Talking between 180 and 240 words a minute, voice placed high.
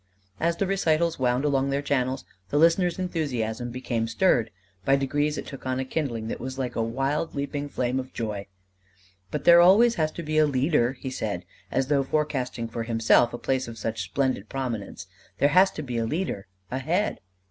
No: average, 195 wpm; low, 135 Hz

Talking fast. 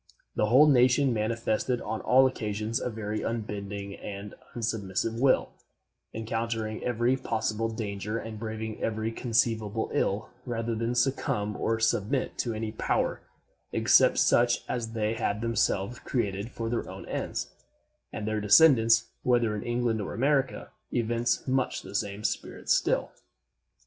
No: average, 140 wpm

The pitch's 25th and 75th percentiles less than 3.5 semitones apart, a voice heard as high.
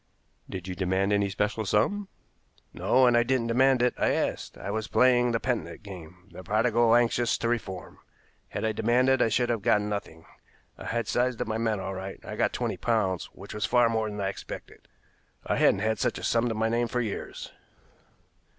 No: average, 3.0 semitones; low, 110 Hz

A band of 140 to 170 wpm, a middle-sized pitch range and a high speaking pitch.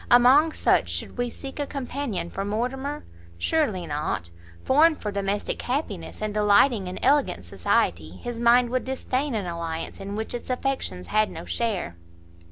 No: average, 160 wpm; wide, 6.1 semitones; high, 230 Hz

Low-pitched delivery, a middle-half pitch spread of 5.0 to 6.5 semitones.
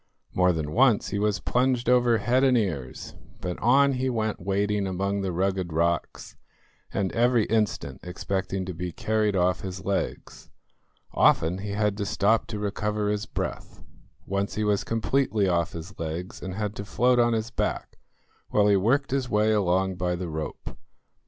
No: low, 100 Hz; average, 3.4 semitones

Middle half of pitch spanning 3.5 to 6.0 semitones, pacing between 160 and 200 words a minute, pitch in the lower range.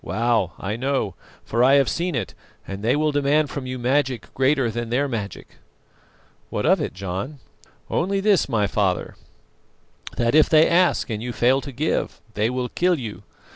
Yes: average, 4.5 semitones; average, 175 wpm; low, 130 Hz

